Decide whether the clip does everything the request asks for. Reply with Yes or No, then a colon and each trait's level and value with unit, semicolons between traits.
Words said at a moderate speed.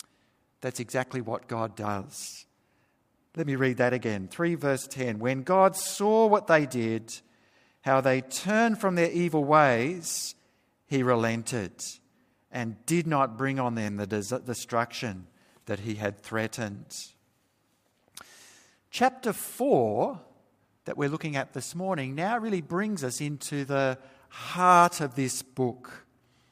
No: slow, 130 wpm